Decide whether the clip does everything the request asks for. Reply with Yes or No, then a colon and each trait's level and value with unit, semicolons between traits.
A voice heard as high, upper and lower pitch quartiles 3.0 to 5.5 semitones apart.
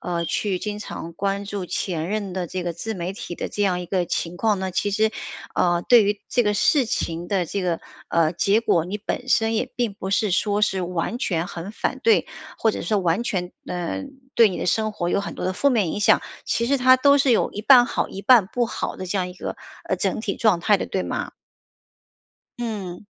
Yes: high, 200 Hz; average, 3.8 semitones